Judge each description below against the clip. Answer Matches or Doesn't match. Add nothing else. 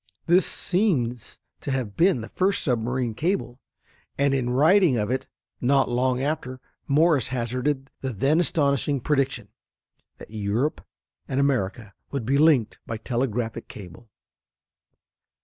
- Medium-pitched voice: Doesn't match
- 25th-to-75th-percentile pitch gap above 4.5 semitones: Doesn't match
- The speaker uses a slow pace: Matches